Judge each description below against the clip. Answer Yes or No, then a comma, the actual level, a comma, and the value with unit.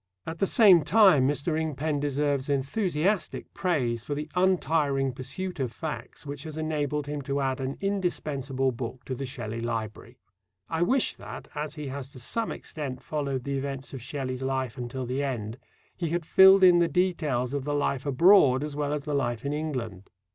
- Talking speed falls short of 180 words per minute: No, average, 185 wpm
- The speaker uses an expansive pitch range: No, average, 3.3 semitones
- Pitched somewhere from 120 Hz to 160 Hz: Yes, medium, 140 Hz